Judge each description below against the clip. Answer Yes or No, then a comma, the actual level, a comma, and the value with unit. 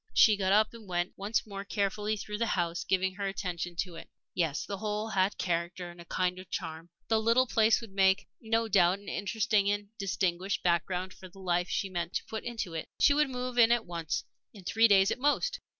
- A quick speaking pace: Yes, fast, 220 wpm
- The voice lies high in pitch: Yes, high, 195 Hz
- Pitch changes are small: No, average, 3.5 semitones